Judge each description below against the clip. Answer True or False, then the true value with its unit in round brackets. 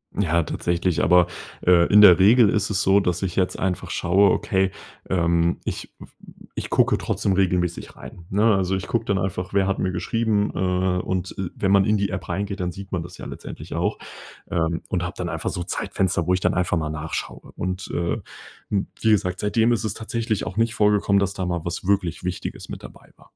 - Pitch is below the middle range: True (95 Hz)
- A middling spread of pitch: False (2.3 semitones)